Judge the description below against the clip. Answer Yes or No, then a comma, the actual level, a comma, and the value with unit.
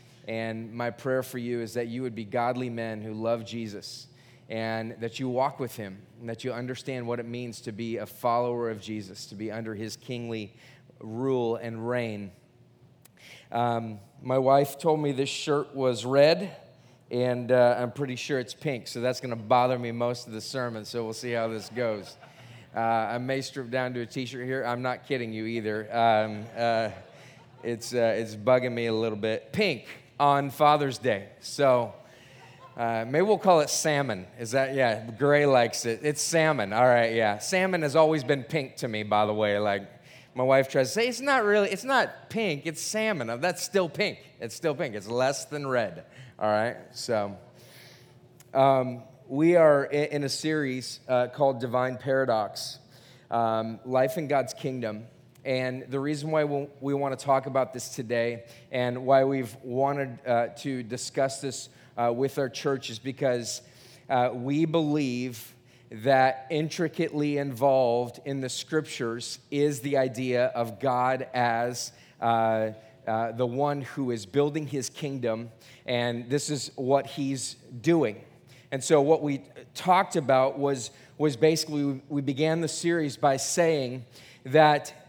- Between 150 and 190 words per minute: Yes, average, 170 wpm